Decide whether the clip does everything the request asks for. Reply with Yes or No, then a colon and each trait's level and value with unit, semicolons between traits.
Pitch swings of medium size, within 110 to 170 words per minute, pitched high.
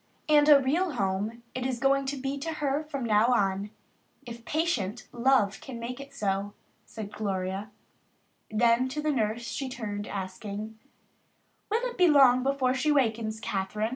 Yes: average, 4.7 semitones; average, 165 wpm; high, 245 Hz